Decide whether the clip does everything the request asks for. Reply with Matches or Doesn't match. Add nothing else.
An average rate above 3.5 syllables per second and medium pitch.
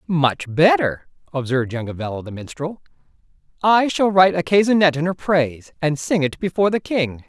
Matches